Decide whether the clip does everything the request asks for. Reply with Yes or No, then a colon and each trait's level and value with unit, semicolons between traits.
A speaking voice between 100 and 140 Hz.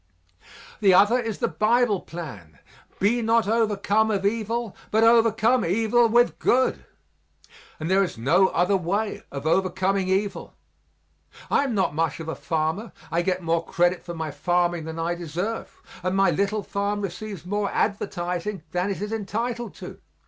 No: high, 195 Hz